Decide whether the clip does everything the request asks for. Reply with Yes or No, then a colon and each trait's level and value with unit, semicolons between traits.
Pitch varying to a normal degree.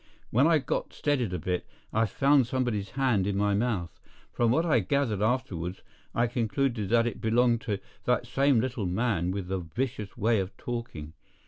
Yes: average, 4.1 semitones